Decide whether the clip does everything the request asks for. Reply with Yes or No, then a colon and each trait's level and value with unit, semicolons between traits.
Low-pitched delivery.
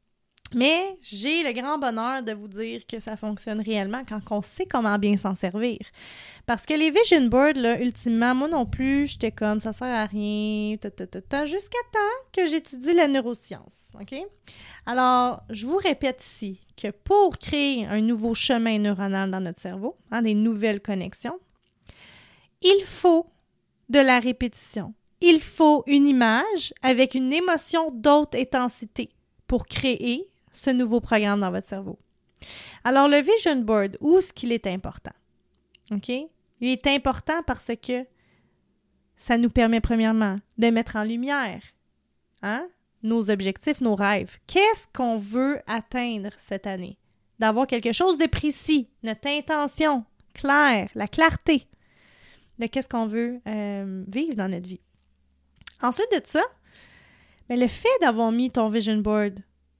No: high, 240 Hz